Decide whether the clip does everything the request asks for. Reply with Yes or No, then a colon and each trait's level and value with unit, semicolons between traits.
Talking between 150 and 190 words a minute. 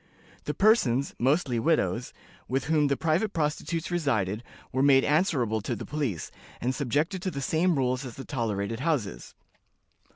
Yes: average, 155 wpm